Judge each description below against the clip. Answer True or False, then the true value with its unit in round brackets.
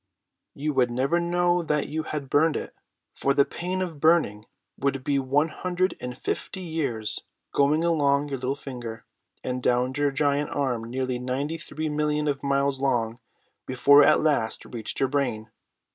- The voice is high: False (140 Hz)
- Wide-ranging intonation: False (3.2 semitones)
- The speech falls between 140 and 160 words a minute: False (170 wpm)